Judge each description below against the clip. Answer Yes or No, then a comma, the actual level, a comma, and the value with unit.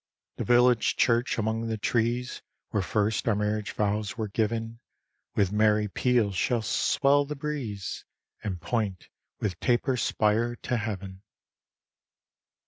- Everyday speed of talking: No, slow, 130 wpm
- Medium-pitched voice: No, low, 110 Hz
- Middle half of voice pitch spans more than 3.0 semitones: No, narrow, 2.4 semitones